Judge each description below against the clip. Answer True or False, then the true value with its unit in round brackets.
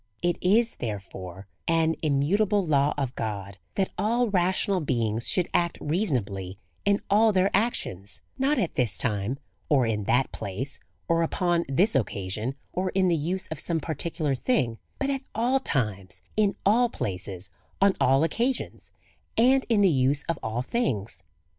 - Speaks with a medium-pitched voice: True (160 Hz)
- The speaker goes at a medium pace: True (160 wpm)